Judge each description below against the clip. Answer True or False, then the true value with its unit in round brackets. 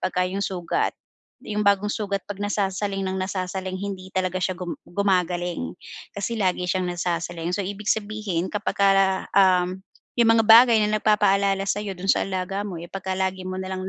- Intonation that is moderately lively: False (1.6 semitones)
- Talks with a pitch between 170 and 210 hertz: True (190 Hz)